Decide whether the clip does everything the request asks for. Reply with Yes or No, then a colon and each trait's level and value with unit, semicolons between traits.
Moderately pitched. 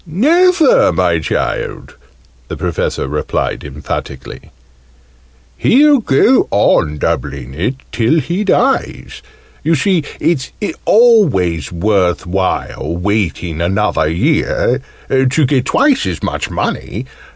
No: low, 110 Hz